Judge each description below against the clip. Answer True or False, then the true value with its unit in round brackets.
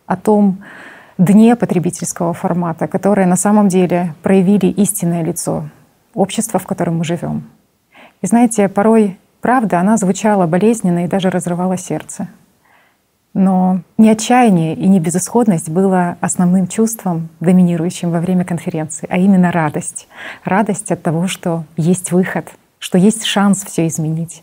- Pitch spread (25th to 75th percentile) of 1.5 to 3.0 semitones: True (2.6 semitones)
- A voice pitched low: False (185 Hz)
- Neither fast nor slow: True (135 wpm)